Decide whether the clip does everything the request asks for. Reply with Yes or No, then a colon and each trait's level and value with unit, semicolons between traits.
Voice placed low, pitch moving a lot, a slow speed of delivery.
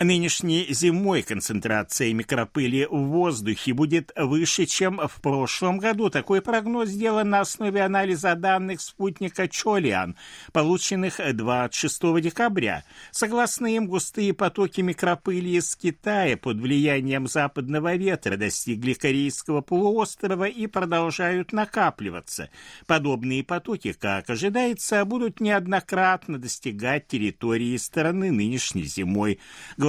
No: medium, 170 Hz; wide, 6.4 semitones; slow, 105 wpm